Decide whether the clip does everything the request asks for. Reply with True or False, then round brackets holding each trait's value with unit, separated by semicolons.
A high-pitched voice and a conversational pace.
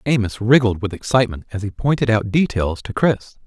False (110 Hz; 190 wpm)